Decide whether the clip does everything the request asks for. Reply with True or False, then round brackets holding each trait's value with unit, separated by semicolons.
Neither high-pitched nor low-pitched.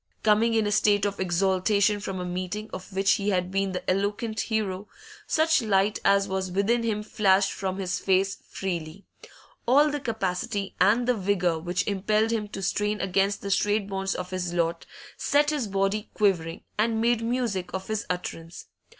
False (200 Hz)